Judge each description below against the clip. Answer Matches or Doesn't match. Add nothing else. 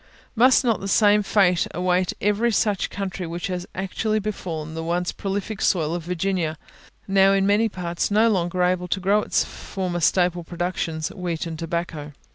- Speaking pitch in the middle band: Matches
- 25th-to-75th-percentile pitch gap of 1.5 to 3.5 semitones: Matches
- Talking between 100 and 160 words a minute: Doesn't match